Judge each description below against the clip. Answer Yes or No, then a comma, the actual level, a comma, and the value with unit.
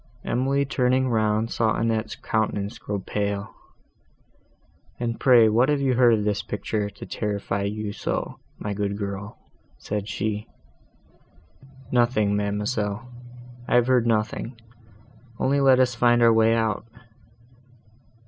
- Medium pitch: No, low, 110 Hz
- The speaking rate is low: Yes, slow, 130 wpm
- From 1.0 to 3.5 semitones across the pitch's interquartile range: Yes, average, 2.9 semitones